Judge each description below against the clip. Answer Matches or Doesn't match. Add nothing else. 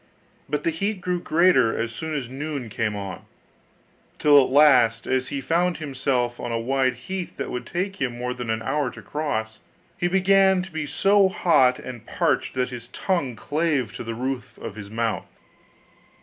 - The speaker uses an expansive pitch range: Matches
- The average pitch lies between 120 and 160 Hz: Matches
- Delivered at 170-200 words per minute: Matches